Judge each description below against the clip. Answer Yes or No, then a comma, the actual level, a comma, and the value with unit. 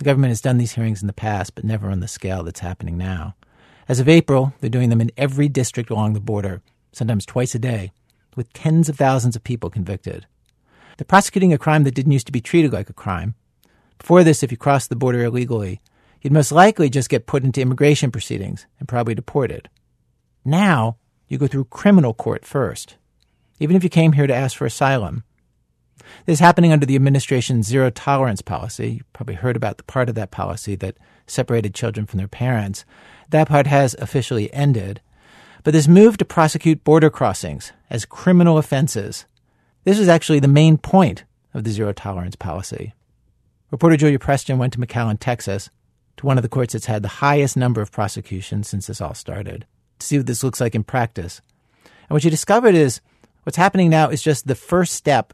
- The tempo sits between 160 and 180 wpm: No, average, 195 wpm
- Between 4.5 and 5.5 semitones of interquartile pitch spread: Yes, average, 5.1 semitones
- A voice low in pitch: Yes, low, 125 Hz